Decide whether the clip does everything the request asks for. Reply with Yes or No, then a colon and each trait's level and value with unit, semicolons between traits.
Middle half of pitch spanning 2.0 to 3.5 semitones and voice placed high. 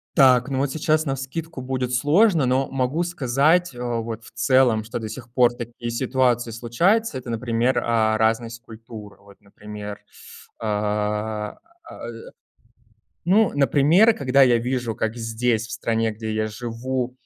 No: average, 3.1 semitones; low, 120 Hz